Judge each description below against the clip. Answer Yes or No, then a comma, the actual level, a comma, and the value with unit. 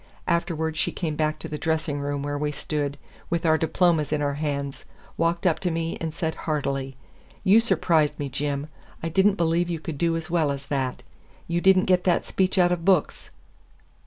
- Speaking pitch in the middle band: Yes, medium, 160 Hz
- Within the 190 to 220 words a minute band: Yes, fast, 205 wpm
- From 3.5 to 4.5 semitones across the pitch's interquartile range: No, average, 2.8 semitones